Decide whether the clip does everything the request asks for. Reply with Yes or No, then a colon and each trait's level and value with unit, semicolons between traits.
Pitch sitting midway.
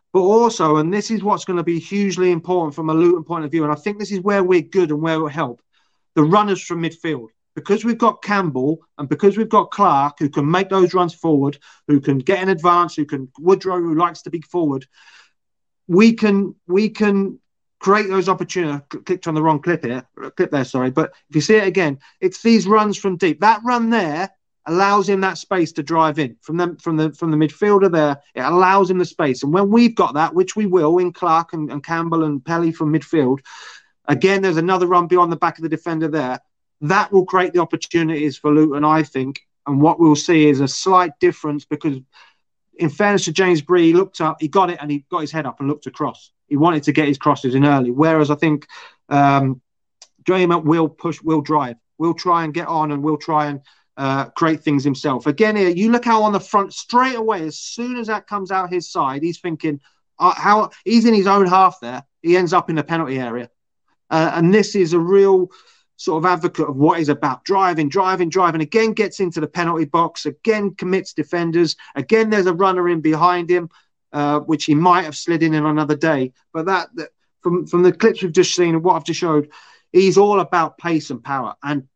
Yes: medium, 170 Hz